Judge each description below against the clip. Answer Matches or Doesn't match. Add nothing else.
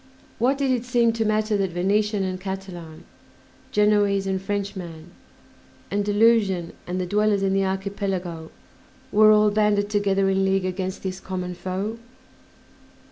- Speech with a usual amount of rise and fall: Doesn't match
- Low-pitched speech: Doesn't match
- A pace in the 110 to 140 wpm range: Matches